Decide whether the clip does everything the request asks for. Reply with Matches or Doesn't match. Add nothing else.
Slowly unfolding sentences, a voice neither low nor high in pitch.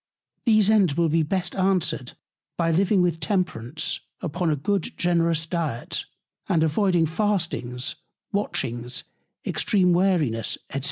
Matches